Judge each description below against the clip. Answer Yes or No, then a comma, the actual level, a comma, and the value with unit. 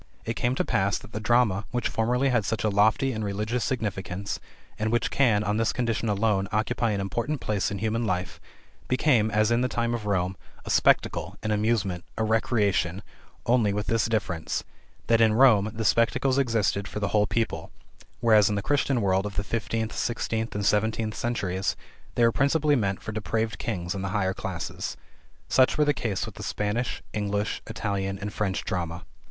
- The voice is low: Yes, low, 110 Hz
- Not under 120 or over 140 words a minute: No, average, 190 wpm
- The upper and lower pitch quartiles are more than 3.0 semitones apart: No, average, 2.7 semitones